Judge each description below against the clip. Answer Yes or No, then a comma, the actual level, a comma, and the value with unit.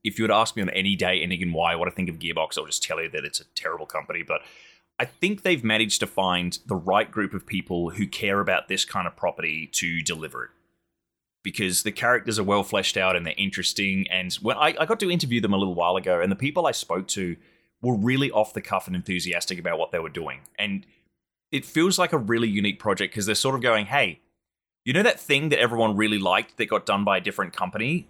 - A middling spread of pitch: Yes, average, 3.7 semitones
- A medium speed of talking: No, fast, 250 wpm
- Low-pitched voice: Yes, low, 100 Hz